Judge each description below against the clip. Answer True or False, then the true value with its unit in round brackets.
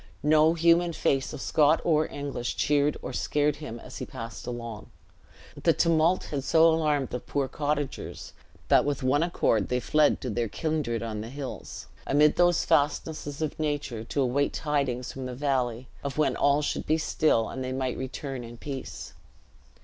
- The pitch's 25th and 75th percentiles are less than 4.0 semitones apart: True (3.4 semitones)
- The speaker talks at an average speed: True (175 wpm)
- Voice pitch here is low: False (145 Hz)